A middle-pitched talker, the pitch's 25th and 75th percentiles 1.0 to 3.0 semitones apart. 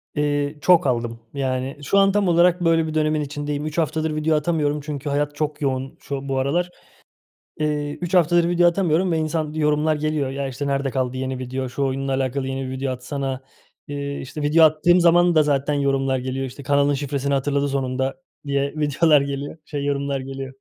Yes: medium, 145 Hz; narrow, 2.4 semitones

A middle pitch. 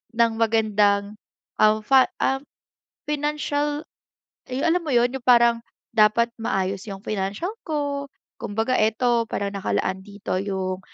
No: high, 225 Hz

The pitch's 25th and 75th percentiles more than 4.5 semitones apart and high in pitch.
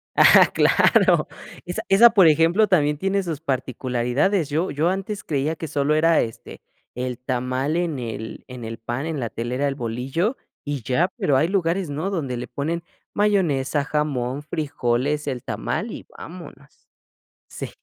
No: average, 4.9 semitones; medium, 145 Hz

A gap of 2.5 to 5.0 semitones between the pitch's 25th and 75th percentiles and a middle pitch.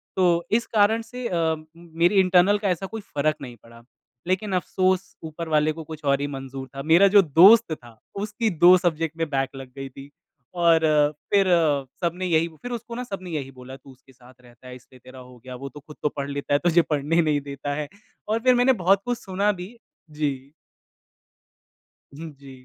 No: wide, 5.5 semitones; medium, 160 Hz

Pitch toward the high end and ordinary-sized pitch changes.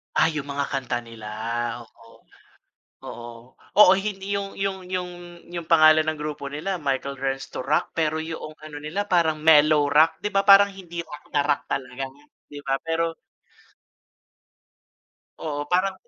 No: medium, 155 Hz; average, 3.9 semitones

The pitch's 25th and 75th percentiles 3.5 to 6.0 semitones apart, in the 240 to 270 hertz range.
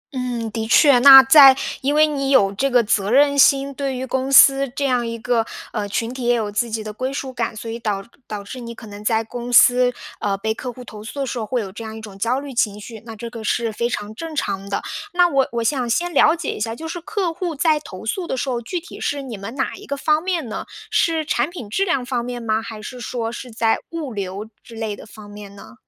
Yes: average, 3.9 semitones; high, 245 Hz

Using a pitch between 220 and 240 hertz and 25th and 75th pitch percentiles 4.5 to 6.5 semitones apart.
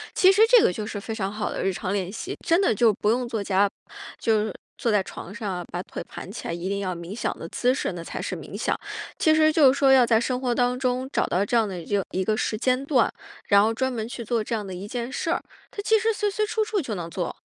Yes: high, 225 Hz; average, 4.8 semitones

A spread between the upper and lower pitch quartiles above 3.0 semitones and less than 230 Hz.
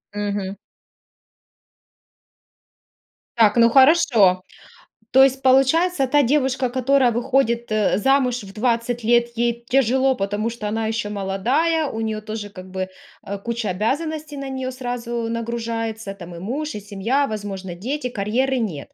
No: average, 4.1 semitones; high, 235 Hz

